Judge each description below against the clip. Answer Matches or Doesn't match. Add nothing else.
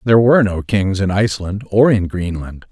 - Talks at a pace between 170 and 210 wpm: Matches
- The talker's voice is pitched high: Doesn't match